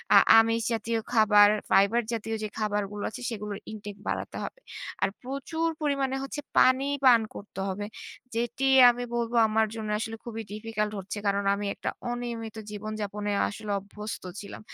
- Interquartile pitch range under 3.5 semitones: Yes, narrow, 2.5 semitones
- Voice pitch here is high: Yes, high, 220 Hz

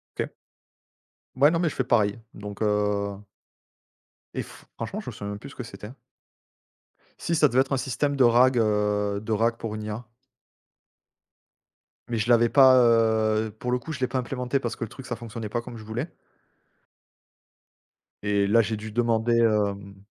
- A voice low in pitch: Yes, low, 115 Hz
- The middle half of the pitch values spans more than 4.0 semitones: No, average, 3.0 semitones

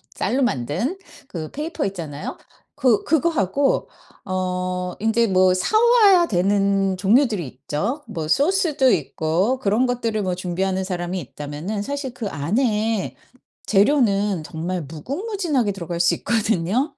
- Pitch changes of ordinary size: No, wide, 6.5 semitones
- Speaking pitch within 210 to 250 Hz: No, high, 200 Hz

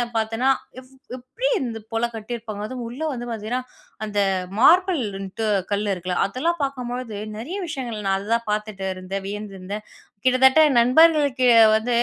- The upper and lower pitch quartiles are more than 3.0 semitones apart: Yes, average, 3.6 semitones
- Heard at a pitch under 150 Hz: No, high, 235 Hz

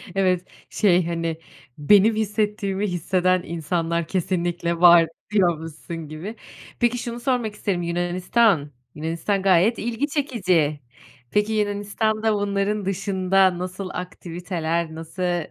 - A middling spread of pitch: Yes, average, 3.5 semitones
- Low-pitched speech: No, medium, 185 Hz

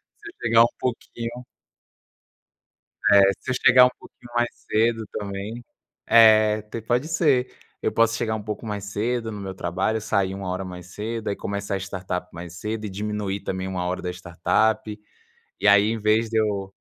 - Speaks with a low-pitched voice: Yes, low, 105 Hz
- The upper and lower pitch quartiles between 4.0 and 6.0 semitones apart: No, average, 2.8 semitones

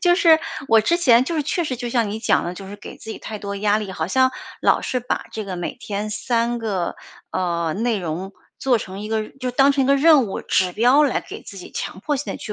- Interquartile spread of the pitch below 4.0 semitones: No, average, 4.8 semitones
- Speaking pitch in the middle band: No, high, 225 Hz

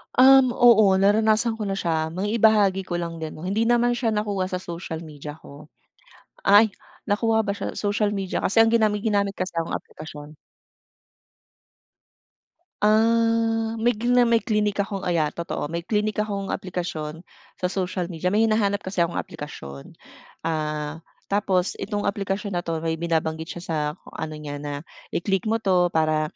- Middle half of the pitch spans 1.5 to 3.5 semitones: No, average, 4.7 semitones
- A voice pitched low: No, high, 195 Hz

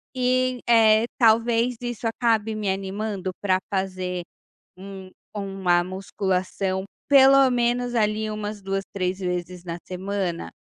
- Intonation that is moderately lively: Yes, average, 3.5 semitones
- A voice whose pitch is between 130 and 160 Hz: No, high, 200 Hz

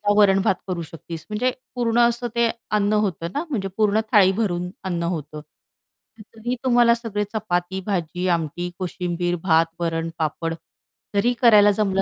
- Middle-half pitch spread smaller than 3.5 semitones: No, average, 4.2 semitones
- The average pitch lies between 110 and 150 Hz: No, high, 195 Hz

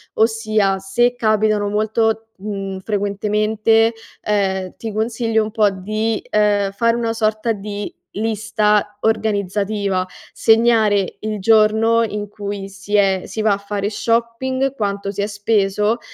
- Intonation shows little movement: Yes, narrow, 1.7 semitones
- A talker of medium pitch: No, high, 210 Hz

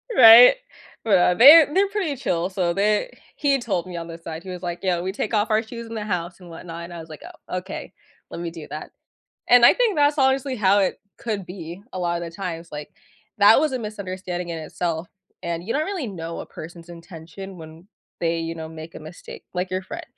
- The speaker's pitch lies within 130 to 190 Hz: Yes, medium, 185 Hz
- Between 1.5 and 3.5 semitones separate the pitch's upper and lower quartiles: No, average, 5.0 semitones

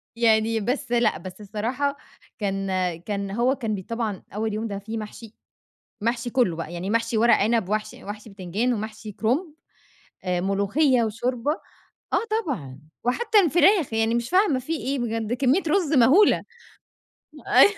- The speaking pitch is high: Yes, high, 230 Hz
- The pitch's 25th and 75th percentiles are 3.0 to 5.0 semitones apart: Yes, average, 3.7 semitones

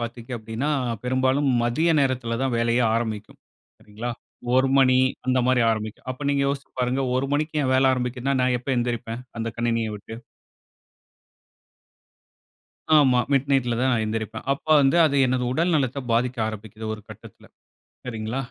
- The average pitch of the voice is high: No, low, 125 Hz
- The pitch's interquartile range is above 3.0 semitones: No, average, 2.7 semitones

